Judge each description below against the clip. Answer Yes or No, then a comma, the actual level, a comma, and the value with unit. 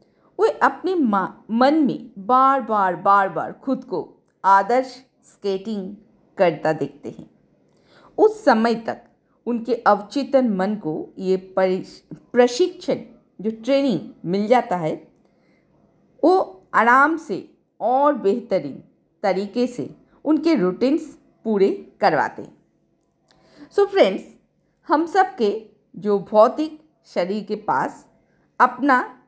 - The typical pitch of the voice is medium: No, high, 235 Hz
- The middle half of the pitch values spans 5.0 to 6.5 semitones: Yes, wide, 5.6 semitones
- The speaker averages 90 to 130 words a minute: Yes, slow, 110 wpm